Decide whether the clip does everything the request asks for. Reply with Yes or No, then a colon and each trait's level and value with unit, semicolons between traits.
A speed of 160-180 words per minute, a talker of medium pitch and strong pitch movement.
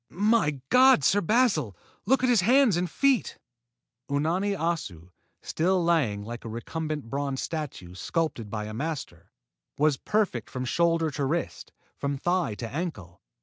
No: average, 145 wpm; medium, 155 Hz; wide, 7.2 semitones